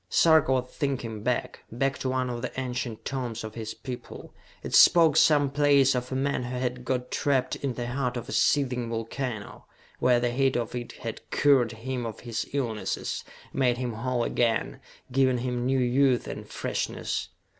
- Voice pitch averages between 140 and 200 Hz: No, low, 125 Hz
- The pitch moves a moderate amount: No, narrow, 1.9 semitones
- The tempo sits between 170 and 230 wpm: Yes, average, 175 wpm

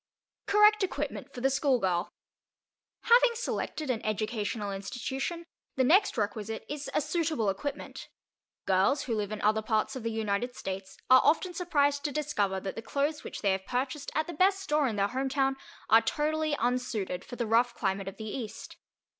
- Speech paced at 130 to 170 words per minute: No, average, 180 wpm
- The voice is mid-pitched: No, very high, 250 Hz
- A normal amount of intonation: No, wide, 6.0 semitones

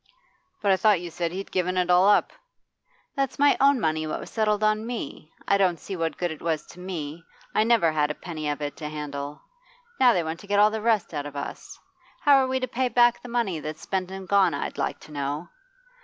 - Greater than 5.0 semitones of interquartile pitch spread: Yes, wide, 5.6 semitones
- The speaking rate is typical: No, fast, 240 wpm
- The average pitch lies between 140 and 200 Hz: Yes, medium, 185 Hz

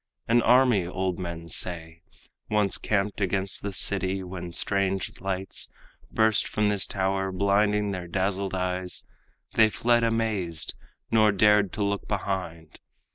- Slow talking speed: Yes, slow, 130 wpm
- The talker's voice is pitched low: Yes, very low, 95 Hz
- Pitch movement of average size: No, narrow, 2.2 semitones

